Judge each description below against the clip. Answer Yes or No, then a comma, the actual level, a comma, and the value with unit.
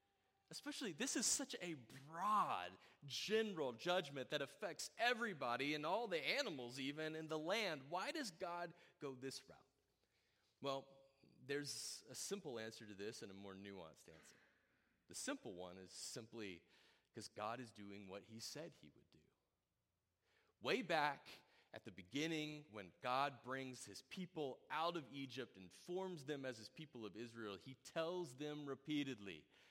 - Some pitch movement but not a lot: No, wide, 6.9 semitones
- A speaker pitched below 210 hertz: Yes, medium, 140 Hz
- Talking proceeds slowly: No, average, 155 wpm